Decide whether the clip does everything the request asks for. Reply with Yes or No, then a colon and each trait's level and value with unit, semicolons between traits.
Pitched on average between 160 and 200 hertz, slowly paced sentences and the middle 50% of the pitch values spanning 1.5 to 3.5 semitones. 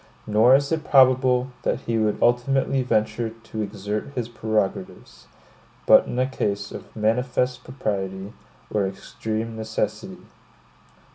No: low, 115 Hz; slow, 125 wpm; average, 2.9 semitones